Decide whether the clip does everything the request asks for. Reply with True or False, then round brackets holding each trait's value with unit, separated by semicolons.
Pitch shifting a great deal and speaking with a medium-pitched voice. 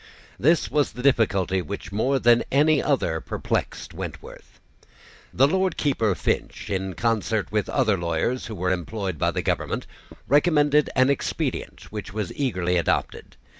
False (6.7 semitones; 115 Hz)